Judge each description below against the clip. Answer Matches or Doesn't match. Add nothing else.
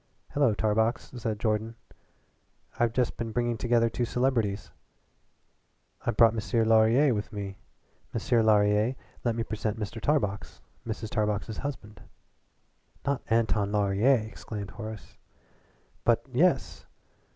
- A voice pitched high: Doesn't match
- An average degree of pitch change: Doesn't match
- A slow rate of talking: Matches